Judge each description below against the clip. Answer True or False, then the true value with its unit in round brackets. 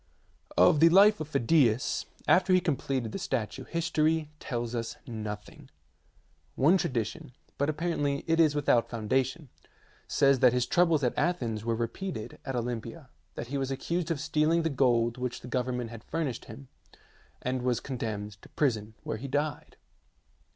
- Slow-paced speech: False (160 wpm)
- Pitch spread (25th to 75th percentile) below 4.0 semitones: False (4.9 semitones)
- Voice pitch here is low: True (130 Hz)